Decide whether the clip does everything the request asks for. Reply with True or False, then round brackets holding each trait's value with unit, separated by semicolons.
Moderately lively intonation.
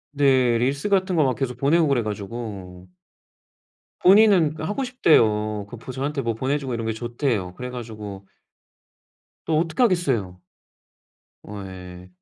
False (6.1 semitones)